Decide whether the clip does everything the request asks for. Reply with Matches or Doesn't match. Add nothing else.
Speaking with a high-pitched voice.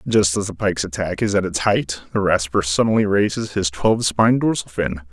Doesn't match